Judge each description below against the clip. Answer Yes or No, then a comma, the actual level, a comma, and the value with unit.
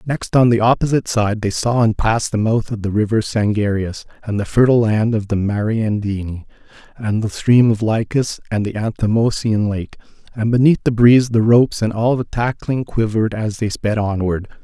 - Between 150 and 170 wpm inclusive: No, average, 190 wpm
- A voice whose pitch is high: No, low, 110 Hz